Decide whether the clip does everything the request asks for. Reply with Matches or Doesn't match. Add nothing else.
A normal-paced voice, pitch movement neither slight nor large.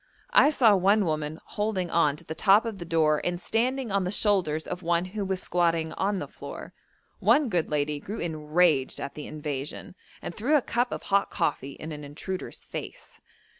Matches